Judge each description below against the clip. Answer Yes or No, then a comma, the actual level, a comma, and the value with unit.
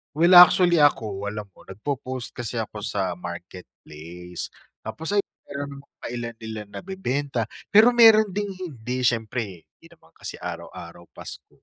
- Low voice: Yes, low, 120 Hz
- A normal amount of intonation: No, wide, 8.3 semitones